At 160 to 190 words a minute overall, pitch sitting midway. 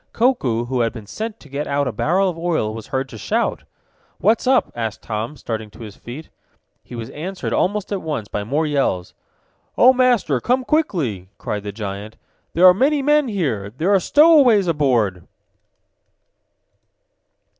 Yes: average, 165 wpm; medium, 145 Hz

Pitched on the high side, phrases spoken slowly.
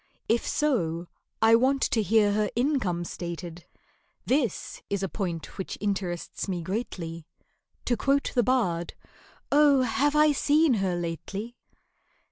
Yes: high, 210 Hz; slow, 130 wpm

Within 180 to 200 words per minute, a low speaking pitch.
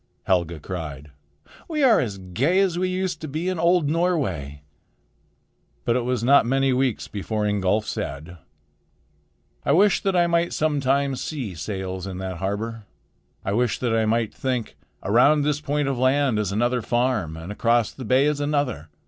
No: average, 170 wpm; low, 125 Hz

